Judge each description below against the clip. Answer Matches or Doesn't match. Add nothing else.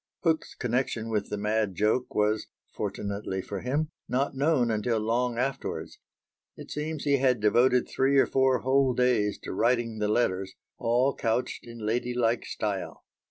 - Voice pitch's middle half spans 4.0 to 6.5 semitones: Doesn't match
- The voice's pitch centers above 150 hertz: Doesn't match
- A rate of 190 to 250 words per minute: Doesn't match